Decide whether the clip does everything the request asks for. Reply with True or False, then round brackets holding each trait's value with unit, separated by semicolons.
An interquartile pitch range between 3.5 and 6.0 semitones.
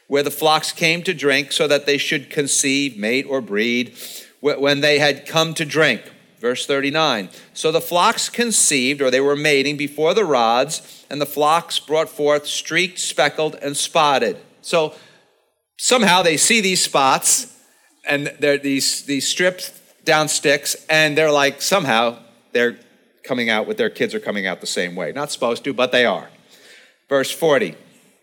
False (2.5 semitones)